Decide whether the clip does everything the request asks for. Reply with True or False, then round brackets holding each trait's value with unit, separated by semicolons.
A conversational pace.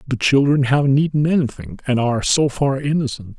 True (195 wpm)